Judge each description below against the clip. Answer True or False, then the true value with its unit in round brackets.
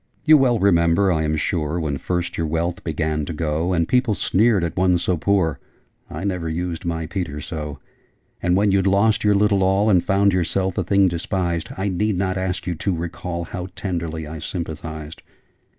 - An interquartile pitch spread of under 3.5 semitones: True (3.0 semitones)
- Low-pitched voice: True (90 Hz)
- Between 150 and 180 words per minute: False (190 wpm)